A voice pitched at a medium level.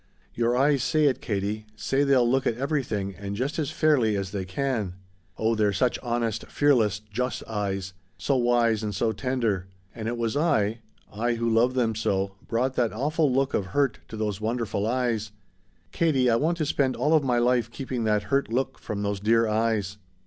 No: low, 115 Hz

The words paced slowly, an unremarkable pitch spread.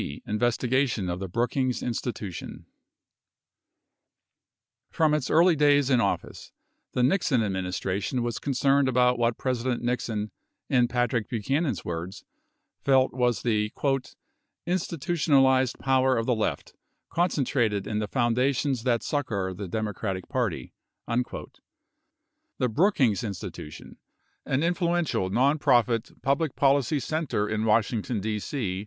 Yes: slow, 120 wpm; average, 4.4 semitones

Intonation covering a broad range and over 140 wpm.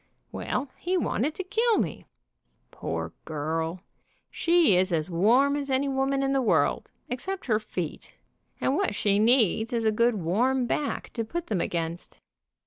Yes: wide, 7.0 semitones; average, 160 wpm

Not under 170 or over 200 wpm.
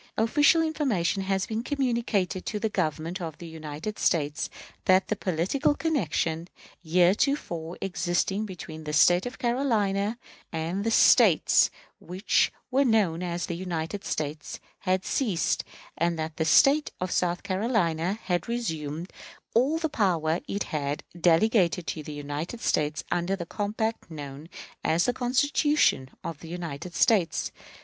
No: average, 140 wpm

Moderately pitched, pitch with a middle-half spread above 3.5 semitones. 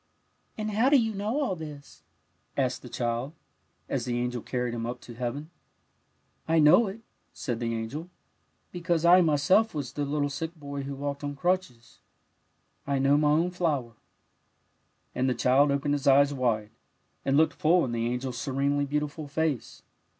Yes: medium, 145 Hz; average, 4.3 semitones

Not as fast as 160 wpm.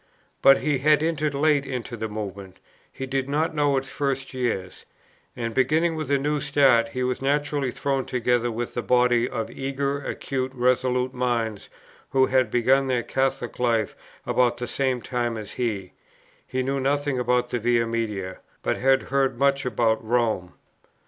No: average, 170 wpm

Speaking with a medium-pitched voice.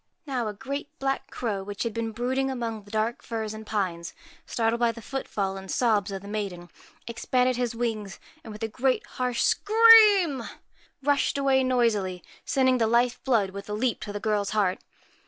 No: high, 230 Hz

